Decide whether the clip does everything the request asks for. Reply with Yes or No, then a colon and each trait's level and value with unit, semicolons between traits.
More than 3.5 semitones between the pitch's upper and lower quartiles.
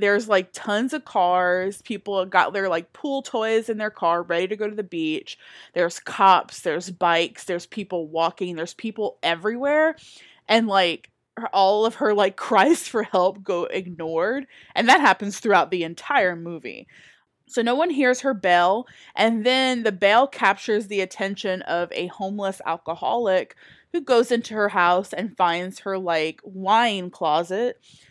Yes: average, 4.0 semitones